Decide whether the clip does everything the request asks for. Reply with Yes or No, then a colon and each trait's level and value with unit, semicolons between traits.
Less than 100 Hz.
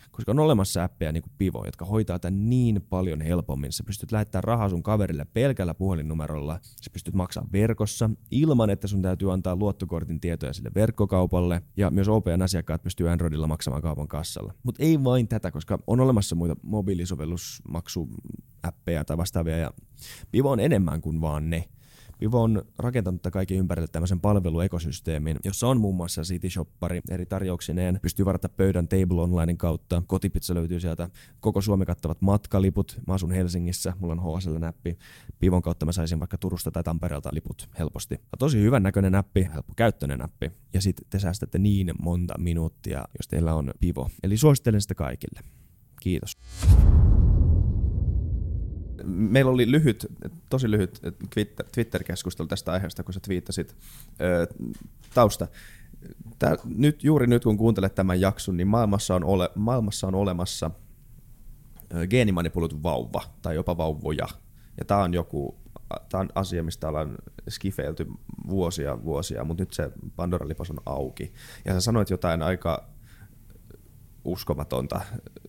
Yes: very low, 90 Hz